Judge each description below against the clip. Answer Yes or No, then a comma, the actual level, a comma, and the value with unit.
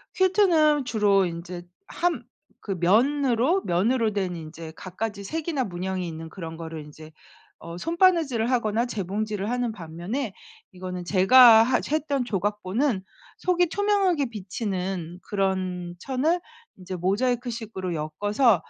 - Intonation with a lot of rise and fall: Yes, wide, 6.3 semitones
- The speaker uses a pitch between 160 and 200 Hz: No, high, 210 Hz